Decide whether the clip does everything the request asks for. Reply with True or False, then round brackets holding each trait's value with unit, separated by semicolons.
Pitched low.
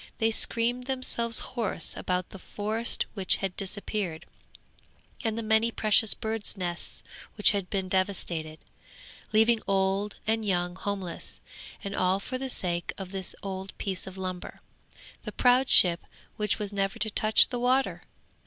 False (200 Hz)